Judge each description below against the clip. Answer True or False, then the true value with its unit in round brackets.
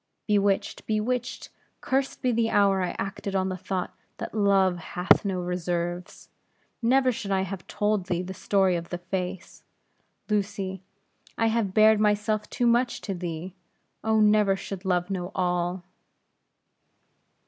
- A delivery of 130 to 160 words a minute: True (145 wpm)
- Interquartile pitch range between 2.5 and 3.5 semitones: True (2.9 semitones)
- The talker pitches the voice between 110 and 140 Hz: False (195 Hz)